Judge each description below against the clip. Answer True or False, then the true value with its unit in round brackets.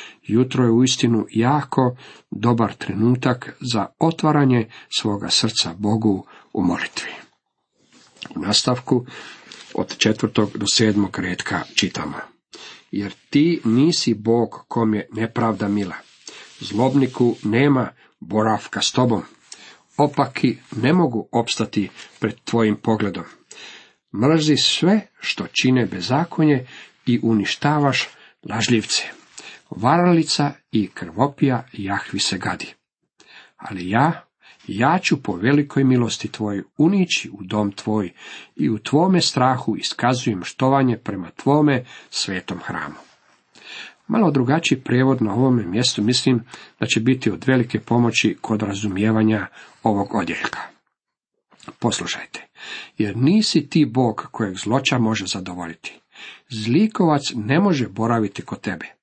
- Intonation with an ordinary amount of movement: True (4.1 semitones)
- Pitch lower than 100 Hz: False (120 Hz)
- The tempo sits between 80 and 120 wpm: True (110 wpm)